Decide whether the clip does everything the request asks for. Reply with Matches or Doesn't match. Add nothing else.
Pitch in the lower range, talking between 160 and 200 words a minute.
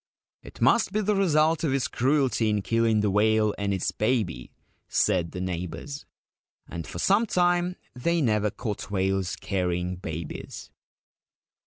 Doesn't match